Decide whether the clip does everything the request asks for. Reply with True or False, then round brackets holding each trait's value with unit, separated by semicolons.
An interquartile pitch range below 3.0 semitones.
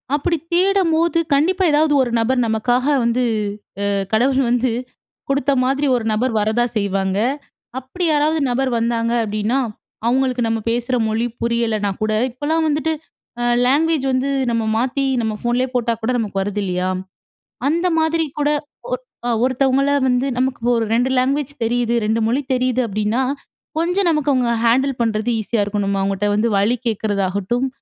False (3.9 semitones)